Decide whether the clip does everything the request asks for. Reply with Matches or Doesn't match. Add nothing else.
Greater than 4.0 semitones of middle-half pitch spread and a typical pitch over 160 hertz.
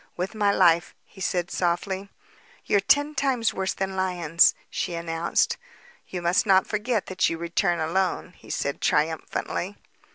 Doesn't match